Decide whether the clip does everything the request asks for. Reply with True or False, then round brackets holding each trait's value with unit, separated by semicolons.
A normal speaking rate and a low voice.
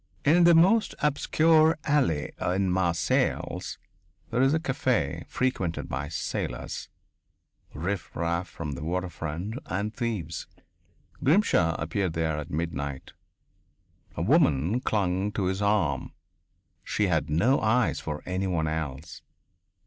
False (120 wpm; 90 Hz)